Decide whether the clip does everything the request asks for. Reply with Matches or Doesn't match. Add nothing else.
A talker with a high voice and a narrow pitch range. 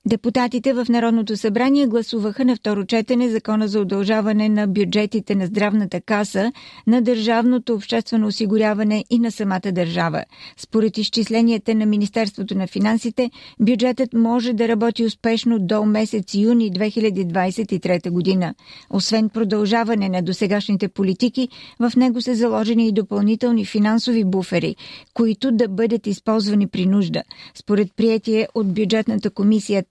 Matches